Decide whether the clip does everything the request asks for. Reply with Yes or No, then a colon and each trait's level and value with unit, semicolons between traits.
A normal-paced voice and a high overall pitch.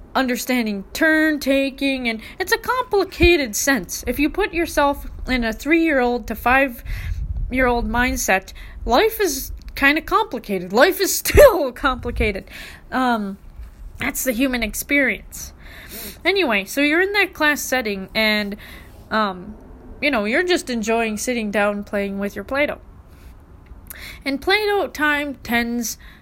No: slow, 125 wpm; very high, 260 Hz